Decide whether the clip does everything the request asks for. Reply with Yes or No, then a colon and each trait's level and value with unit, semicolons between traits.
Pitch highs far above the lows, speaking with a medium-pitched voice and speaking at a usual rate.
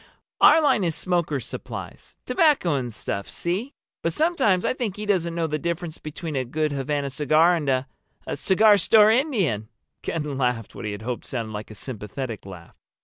Yes: wide, 6.8 semitones; medium, 155 Hz; average, 170 wpm